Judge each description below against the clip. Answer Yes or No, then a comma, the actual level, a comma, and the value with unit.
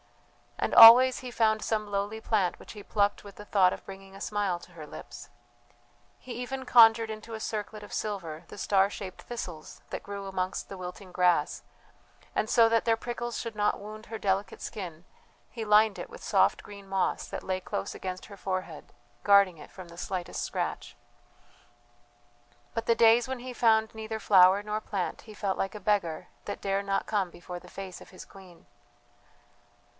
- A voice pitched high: Yes, high, 205 Hz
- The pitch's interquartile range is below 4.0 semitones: Yes, average, 2.8 semitones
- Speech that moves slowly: No, average, 185 wpm